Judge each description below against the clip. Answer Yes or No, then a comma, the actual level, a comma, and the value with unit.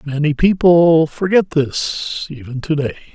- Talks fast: No, slow, 135 wpm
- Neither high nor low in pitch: Yes, medium, 155 Hz